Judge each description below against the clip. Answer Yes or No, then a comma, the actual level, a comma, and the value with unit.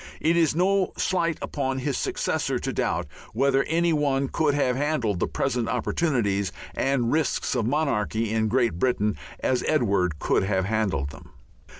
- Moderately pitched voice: No, low, 130 Hz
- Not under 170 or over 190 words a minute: No, average, 160 wpm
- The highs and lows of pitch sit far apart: Yes, wide, 5.9 semitones